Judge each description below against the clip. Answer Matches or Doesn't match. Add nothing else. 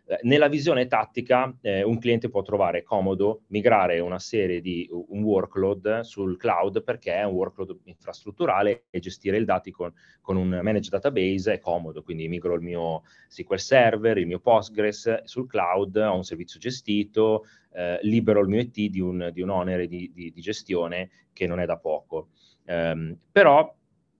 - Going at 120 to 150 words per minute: Doesn't match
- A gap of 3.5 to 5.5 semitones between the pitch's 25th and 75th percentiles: Matches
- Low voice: Matches